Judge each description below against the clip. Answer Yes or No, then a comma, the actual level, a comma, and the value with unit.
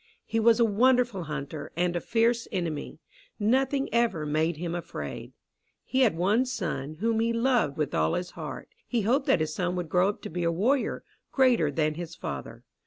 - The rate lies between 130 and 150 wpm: No, average, 190 wpm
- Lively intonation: Yes, wide, 6.7 semitones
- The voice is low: No, medium, 185 Hz